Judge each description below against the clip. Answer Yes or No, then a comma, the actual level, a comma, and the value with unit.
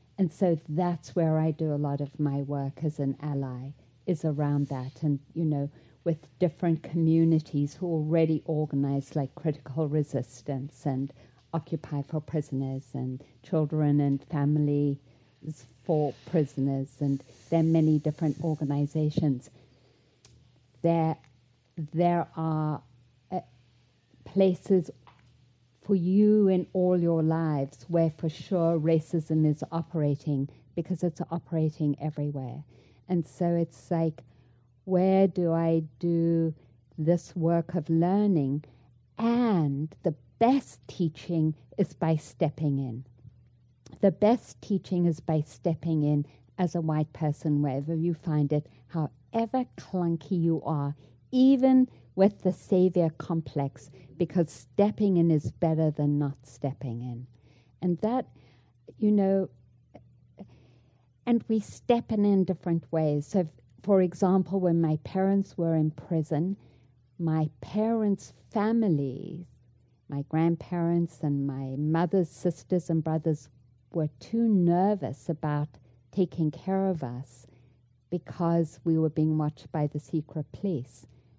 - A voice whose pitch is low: No, medium, 155 Hz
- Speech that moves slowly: Yes, slow, 125 wpm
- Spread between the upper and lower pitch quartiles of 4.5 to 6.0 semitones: No, average, 4.1 semitones